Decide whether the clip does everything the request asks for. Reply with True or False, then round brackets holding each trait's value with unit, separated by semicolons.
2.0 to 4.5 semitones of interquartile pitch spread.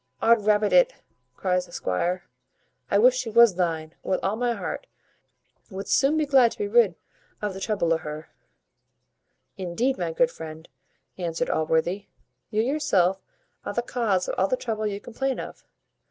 False (5.2 semitones)